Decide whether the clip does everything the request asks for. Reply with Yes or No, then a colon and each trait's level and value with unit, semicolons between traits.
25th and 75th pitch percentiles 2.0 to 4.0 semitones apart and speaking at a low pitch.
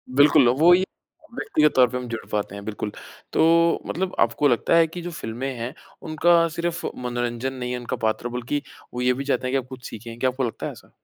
No: average, 5.1 semitones; low, 130 Hz